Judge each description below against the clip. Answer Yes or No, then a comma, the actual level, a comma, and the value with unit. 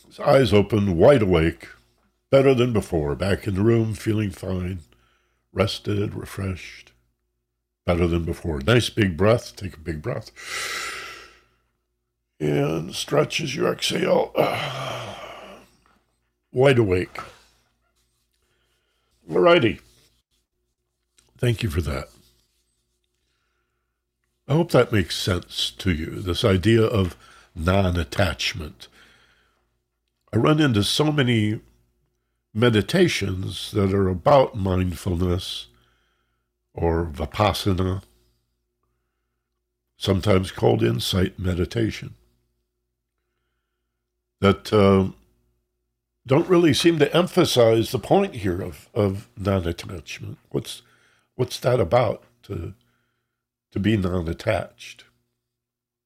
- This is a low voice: Yes, very low, 90 Hz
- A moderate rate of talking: No, slow, 90 wpm